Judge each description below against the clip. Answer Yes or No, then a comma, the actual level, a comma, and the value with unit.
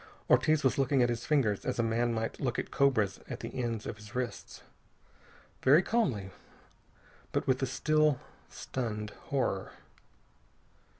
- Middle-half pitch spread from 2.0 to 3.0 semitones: No, average, 3.6 semitones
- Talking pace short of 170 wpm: Yes, average, 145 wpm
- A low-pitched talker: Yes, low, 125 Hz